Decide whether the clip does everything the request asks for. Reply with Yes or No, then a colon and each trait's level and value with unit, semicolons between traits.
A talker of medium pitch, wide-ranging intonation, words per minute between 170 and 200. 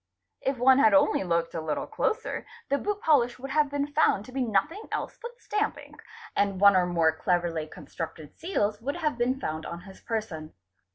No: high, 235 Hz; wide, 8.8 semitones; average, 195 wpm